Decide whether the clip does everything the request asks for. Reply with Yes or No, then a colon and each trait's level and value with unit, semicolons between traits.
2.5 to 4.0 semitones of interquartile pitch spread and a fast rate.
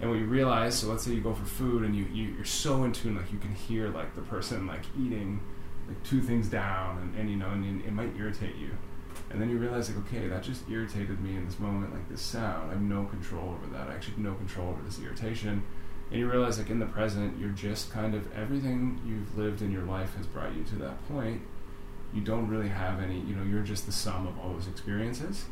Yes: average, 3.0 semitones; fast, 255 wpm